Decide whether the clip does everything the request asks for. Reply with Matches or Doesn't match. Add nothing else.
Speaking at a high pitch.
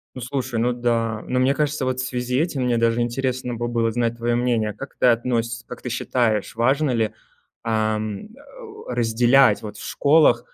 Doesn't match